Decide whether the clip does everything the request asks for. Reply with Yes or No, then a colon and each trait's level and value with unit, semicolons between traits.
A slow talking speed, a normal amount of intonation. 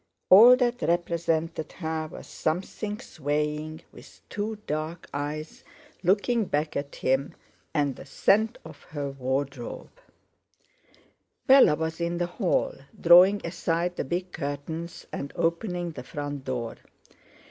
Yes: slow, 125 wpm; average, 3.6 semitones